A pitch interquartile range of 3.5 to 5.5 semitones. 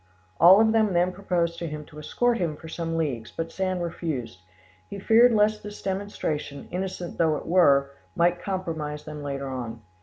Yes: average, 4.3 semitones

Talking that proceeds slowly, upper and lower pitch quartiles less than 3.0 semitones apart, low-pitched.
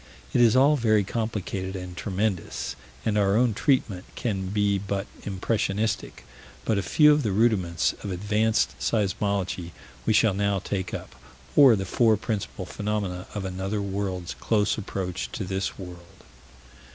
No: average, 150 wpm; narrow, 2.5 semitones; low, 100 Hz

